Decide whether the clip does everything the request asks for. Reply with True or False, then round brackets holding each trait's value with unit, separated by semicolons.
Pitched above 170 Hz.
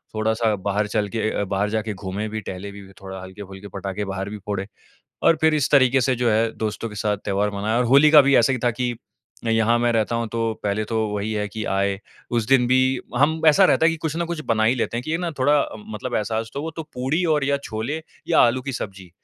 False (110 Hz)